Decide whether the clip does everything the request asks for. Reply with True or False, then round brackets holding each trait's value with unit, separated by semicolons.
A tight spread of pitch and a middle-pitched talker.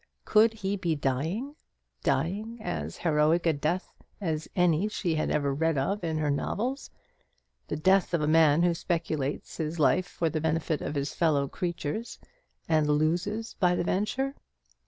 False (4.0 semitones; 165 Hz)